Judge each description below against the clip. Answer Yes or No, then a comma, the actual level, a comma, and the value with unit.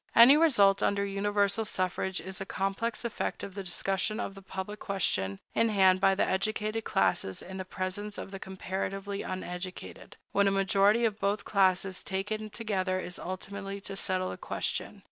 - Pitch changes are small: Yes, narrow, 1.6 semitones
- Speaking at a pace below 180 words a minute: Yes, average, 170 wpm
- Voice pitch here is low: No, high, 195 Hz